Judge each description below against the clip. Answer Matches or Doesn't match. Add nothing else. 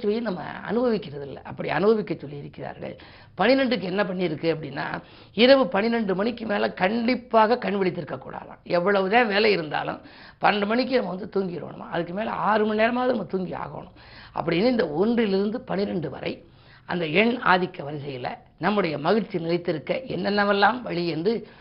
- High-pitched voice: Matches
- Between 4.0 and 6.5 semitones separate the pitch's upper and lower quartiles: Matches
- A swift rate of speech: Matches